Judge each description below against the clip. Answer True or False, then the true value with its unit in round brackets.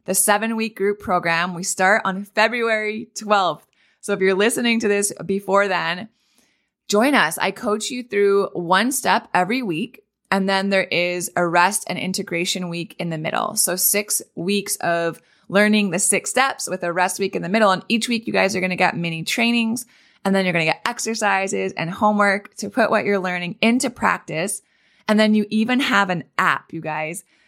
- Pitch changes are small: False (3.3 semitones)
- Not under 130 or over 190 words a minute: False (200 wpm)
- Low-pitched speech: False (200 Hz)